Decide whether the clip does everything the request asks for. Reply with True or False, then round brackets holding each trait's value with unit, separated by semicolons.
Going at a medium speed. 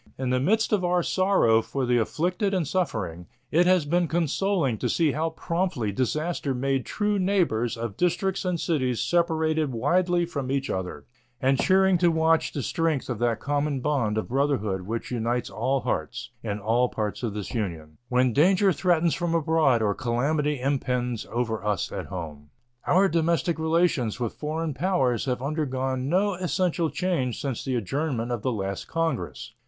True (170 wpm)